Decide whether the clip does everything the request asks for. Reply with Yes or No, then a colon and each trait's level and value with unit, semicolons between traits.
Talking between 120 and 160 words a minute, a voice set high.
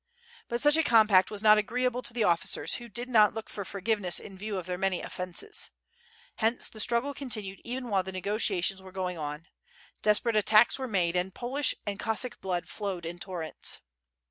No: average, 195 wpm; high, 210 Hz